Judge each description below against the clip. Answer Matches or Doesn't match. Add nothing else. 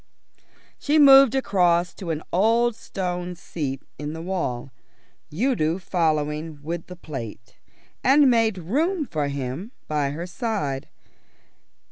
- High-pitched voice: Doesn't match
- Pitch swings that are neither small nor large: Doesn't match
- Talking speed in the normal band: Doesn't match